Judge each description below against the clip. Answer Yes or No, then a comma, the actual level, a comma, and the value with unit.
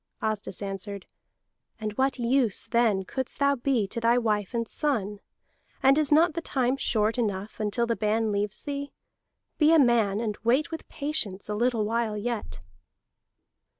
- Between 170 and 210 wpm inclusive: No, average, 160 wpm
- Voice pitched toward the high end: Yes, high, 230 Hz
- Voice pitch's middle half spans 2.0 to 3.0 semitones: No, average, 4.2 semitones